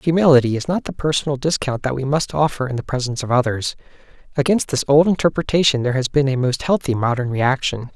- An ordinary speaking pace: Yes, average, 195 wpm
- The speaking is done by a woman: No, male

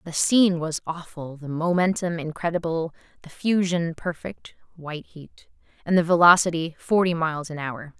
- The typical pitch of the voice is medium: Yes, medium, 165 Hz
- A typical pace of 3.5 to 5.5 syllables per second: Yes, 5.2 syllables/s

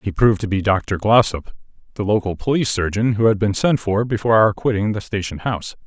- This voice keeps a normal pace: No, fast, 215 wpm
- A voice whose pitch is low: Yes, low, 105 Hz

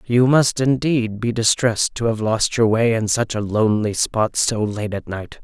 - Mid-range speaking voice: No, low, 115 Hz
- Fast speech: Yes, fast, 210 wpm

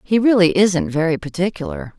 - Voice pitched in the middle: Yes, medium, 165 Hz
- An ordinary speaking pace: Yes, average, 150 wpm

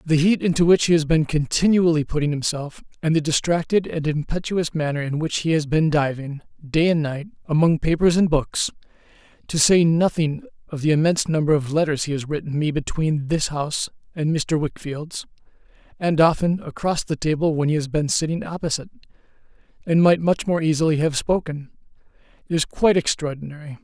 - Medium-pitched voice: Yes, medium, 155 Hz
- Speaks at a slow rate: No, average, 175 wpm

